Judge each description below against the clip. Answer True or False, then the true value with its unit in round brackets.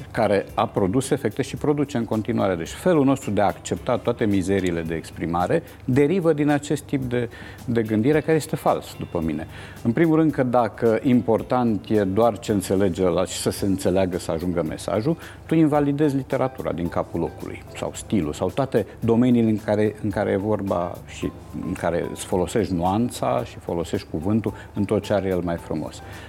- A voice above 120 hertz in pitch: False (110 Hz)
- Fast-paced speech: True (185 wpm)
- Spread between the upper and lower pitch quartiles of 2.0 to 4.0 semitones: False (4.9 semitones)